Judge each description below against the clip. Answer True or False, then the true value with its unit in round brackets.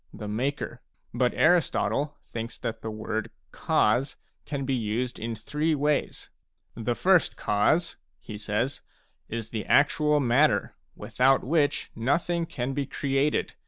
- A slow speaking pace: False (160 wpm)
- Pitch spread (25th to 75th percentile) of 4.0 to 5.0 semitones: True (4.7 semitones)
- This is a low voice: True (130 Hz)